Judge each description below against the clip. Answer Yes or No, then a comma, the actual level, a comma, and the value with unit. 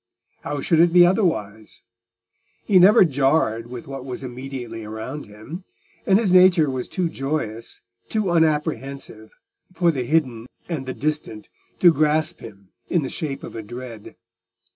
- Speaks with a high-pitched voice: No, medium, 140 Hz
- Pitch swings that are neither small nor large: No, wide, 6.1 semitones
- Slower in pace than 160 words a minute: Yes, average, 150 wpm